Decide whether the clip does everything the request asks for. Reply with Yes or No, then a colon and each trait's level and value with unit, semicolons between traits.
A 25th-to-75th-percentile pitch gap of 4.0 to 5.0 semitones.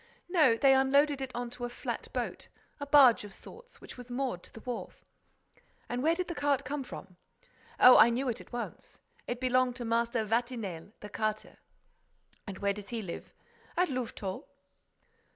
No: average, 3.2 semitones